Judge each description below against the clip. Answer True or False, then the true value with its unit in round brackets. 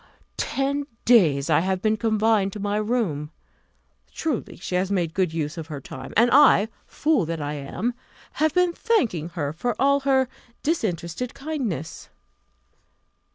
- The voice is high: True (210 Hz)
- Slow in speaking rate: False (155 wpm)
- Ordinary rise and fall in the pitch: False (8.2 semitones)